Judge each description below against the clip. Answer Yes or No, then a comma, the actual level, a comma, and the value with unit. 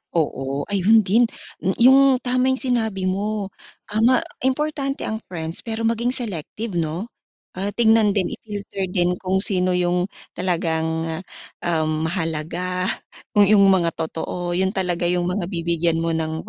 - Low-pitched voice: No, medium, 185 Hz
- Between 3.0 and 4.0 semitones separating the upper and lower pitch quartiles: No, average, 4.4 semitones